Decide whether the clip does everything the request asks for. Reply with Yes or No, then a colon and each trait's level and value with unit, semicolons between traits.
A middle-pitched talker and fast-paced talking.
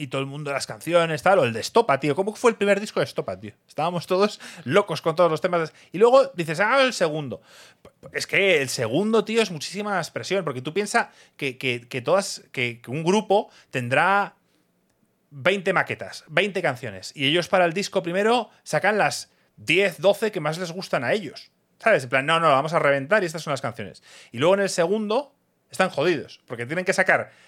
Yes: medium, 180 Hz; fast, 210 wpm